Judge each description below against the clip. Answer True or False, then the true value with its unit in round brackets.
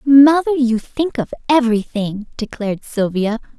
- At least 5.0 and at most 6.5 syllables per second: False (4.8 syllables/s)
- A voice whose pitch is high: True (245 Hz)